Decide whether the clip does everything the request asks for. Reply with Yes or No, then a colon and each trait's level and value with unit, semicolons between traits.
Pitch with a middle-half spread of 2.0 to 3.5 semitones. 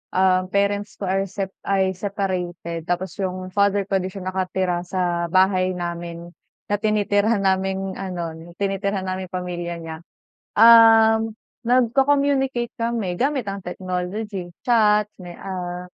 Yes: narrow, 2.5 semitones